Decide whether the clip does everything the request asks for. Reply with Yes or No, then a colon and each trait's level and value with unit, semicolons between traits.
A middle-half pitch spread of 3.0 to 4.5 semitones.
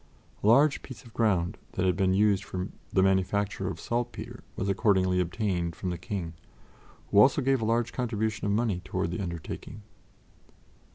Yes: average, 3.5 semitones